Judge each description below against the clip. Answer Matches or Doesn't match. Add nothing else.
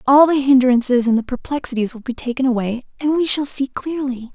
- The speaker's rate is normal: Matches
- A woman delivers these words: Matches